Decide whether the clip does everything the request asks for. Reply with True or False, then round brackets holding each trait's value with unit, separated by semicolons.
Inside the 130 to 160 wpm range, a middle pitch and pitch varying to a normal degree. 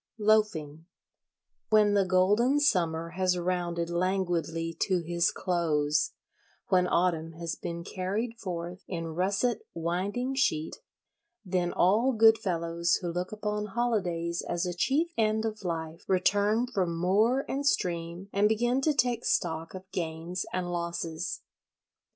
True (135 wpm; 180 Hz; 4.1 semitones)